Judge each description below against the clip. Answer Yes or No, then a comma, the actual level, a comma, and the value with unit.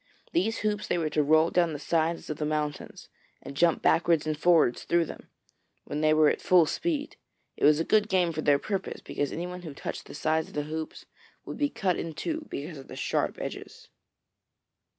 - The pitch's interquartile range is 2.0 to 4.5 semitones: Yes, average, 2.9 semitones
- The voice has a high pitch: No, medium, 160 Hz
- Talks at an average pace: No, fast, 210 wpm